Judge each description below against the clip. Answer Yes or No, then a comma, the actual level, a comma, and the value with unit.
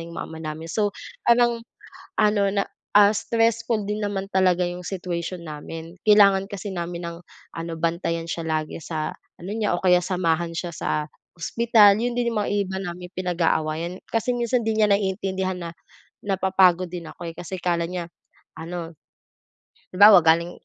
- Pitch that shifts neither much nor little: Yes, average, 3.3 semitones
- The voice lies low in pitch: No, medium, 185 Hz